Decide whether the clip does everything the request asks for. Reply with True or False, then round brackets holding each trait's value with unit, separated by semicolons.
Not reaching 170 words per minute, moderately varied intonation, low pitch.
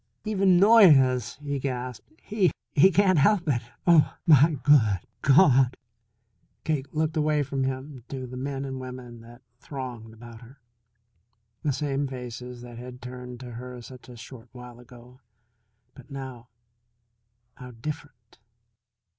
True (145 wpm; 3.1 semitones; 130 Hz)